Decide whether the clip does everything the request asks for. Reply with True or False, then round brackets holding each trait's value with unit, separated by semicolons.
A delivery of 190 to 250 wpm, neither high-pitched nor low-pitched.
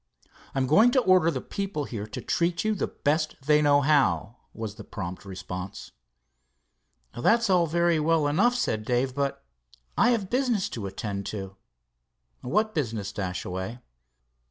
False (155 wpm; 145 Hz)